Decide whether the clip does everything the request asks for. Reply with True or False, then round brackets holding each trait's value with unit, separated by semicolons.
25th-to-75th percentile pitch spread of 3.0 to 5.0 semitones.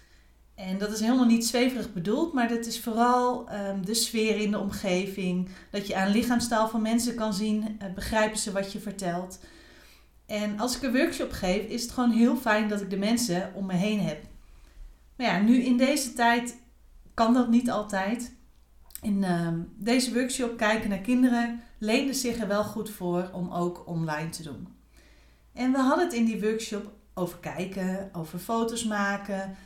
True (3.5 semitones)